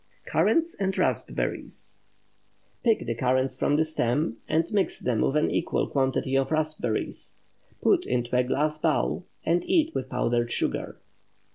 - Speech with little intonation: No, average, 4.6 semitones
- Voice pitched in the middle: Yes, medium, 145 Hz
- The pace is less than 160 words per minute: Yes, average, 140 wpm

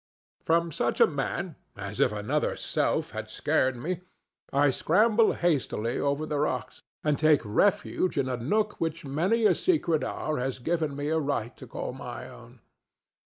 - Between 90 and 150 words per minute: No, average, 165 wpm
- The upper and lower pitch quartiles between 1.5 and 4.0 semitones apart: No, average, 4.8 semitones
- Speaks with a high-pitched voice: No, medium, 150 Hz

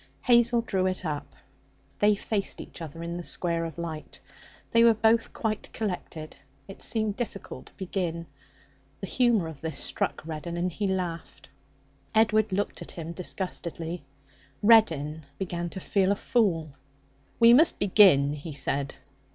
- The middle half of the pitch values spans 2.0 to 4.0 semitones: No, average, 4.7 semitones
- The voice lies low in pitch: No, medium, 185 Hz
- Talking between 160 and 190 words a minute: No, average, 150 wpm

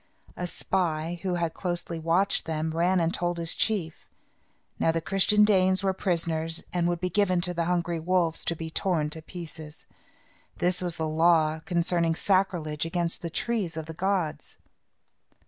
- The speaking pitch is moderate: Yes, medium, 170 Hz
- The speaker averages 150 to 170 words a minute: Yes, average, 165 wpm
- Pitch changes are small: Yes, narrow, 2.1 semitones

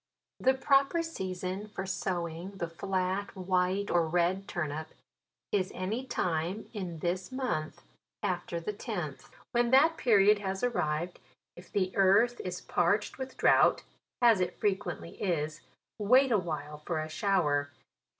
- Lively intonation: No, average, 3.6 semitones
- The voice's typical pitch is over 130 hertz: Yes, medium, 185 Hz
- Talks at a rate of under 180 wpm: Yes, average, 140 wpm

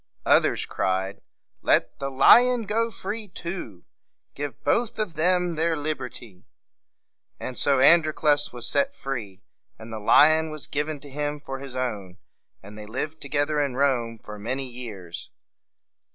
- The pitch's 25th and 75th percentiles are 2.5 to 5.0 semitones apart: No, wide, 5.4 semitones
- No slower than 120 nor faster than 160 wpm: Yes, average, 145 wpm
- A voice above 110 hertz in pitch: Yes, medium, 140 Hz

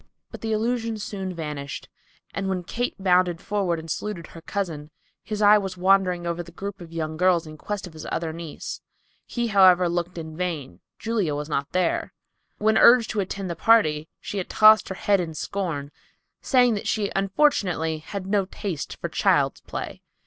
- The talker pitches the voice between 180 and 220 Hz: Yes, medium, 185 Hz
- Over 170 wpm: Yes, average, 185 wpm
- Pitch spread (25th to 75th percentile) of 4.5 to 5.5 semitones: No, average, 3.9 semitones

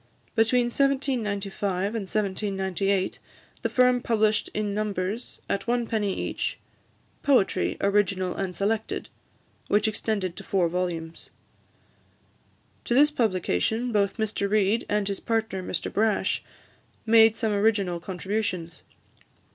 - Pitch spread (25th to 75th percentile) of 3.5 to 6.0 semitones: No, average, 2.8 semitones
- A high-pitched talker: Yes, high, 205 Hz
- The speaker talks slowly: Yes, slow, 115 wpm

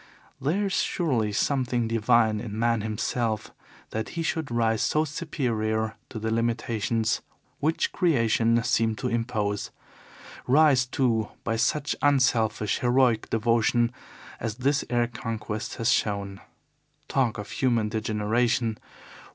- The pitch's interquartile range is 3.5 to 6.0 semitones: No, average, 2.7 semitones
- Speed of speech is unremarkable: No, slow, 120 wpm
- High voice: No, low, 115 Hz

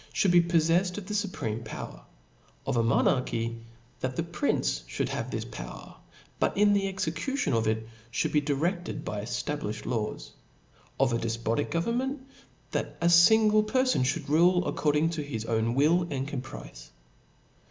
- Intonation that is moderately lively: No, wide, 7.9 semitones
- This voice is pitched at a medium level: Yes, medium, 150 Hz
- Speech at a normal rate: Yes, average, 155 wpm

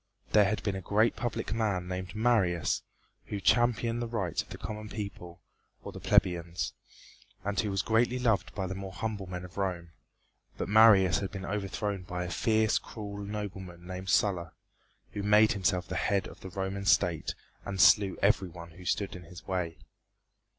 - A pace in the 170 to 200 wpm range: Yes, average, 180 wpm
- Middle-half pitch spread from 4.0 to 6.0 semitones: No, average, 2.7 semitones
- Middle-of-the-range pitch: No, low, 100 Hz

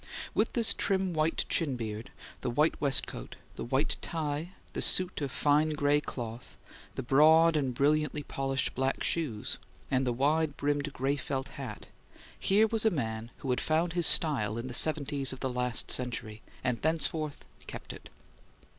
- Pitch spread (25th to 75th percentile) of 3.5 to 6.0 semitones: Yes, average, 3.8 semitones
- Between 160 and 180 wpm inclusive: Yes, average, 165 wpm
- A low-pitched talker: No, medium, 145 Hz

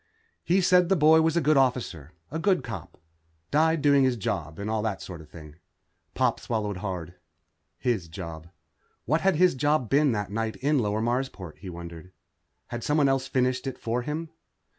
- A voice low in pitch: Yes, low, 125 Hz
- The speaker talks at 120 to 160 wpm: No, average, 185 wpm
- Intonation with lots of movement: Yes, wide, 7.9 semitones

